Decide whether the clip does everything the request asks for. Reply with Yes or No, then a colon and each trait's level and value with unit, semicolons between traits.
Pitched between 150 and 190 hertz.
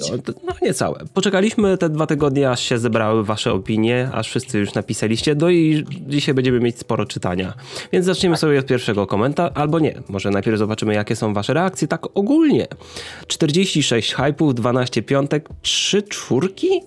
No: low, 135 Hz